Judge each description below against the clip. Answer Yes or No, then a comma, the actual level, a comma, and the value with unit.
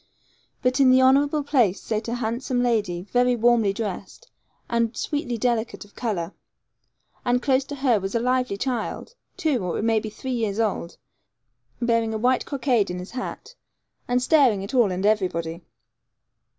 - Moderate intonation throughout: Yes, average, 3.5 semitones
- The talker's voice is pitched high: Yes, high, 235 Hz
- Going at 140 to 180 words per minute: Yes, average, 165 wpm